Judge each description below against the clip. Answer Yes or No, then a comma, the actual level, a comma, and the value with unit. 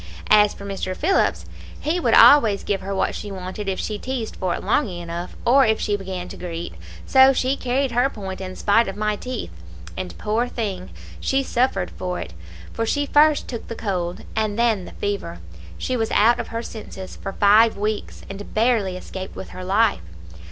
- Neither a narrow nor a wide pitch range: Yes, average, 4.0 semitones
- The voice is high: Yes, high, 210 Hz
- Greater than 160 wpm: Yes, average, 195 wpm